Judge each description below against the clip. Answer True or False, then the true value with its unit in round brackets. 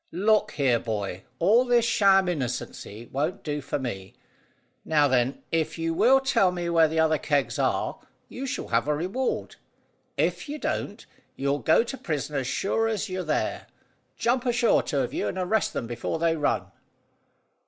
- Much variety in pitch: True (7.6 semitones)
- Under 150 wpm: False (175 wpm)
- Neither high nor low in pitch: True (160 Hz)